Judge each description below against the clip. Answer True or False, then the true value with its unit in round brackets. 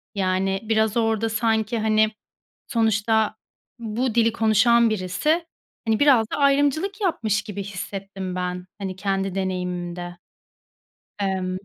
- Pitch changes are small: False (3.1 semitones)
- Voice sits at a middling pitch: False (215 Hz)